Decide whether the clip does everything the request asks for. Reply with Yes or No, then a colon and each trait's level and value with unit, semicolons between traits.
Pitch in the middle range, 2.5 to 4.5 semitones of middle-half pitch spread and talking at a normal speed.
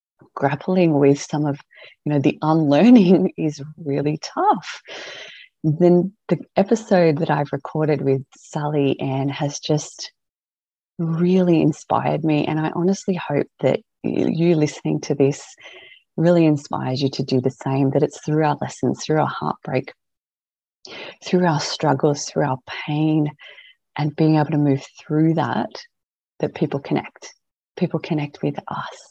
Yes: medium, 150 Hz; average, 2.8 semitones; average, 145 wpm